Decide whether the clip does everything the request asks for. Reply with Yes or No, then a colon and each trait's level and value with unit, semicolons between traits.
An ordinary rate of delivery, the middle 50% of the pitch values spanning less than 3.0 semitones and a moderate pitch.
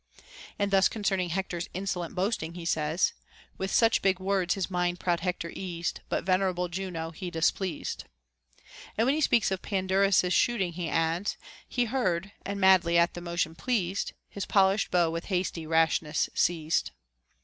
Yes: average, 170 wpm; narrow, 2.4 semitones; medium, 180 Hz